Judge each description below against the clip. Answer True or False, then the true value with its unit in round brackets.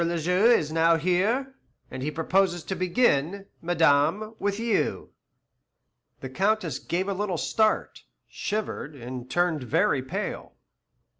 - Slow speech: True (130 wpm)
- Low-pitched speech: False (175 Hz)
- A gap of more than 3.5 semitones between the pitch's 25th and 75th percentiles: True (4.9 semitones)